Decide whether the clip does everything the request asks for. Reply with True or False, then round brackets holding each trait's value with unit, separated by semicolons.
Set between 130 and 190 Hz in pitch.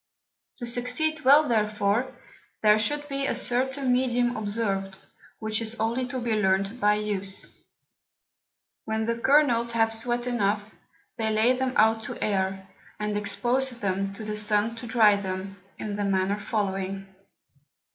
False (220 Hz)